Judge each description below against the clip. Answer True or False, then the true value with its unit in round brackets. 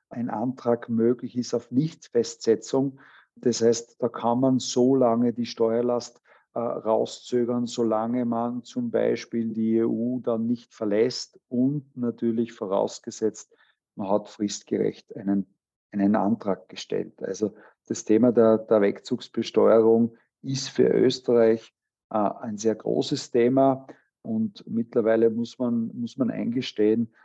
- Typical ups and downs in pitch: False (1.9 semitones)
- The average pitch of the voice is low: True (120 Hz)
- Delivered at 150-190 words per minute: False (125 wpm)